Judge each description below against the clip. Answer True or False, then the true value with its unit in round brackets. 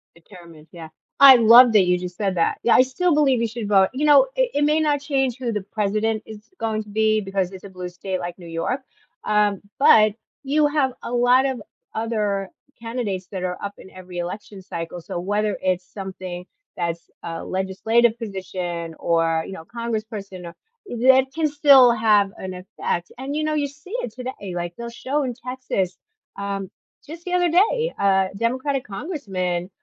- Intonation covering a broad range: True (5.8 semitones)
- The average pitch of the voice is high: True (215 Hz)